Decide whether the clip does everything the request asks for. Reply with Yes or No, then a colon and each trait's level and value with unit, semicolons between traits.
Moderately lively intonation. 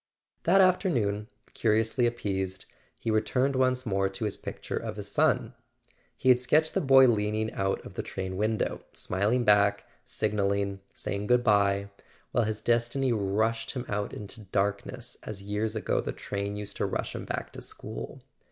Yes: average, 3.3 semitones